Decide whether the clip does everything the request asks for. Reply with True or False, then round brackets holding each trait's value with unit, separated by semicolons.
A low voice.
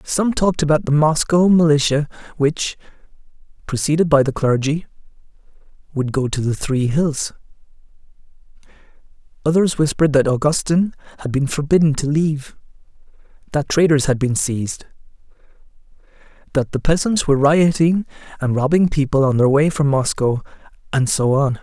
False (145 Hz)